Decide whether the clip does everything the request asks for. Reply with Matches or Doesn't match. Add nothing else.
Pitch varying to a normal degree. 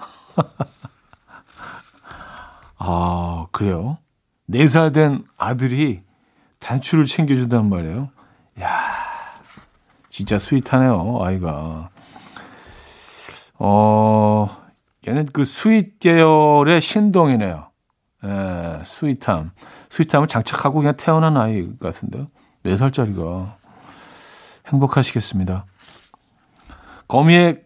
Doesn't match